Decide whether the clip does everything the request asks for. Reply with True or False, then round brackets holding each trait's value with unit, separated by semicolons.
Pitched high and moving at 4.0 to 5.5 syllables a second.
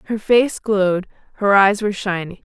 True (200 Hz; 5.2 syllables/s)